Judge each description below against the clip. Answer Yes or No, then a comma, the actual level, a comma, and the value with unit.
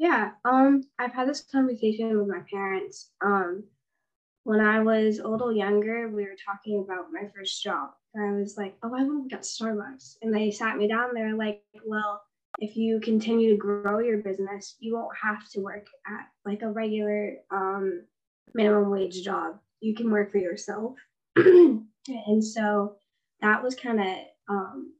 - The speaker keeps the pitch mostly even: Yes, narrow, 2.1 semitones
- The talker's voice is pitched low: No, high, 215 Hz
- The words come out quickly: No, average, 180 wpm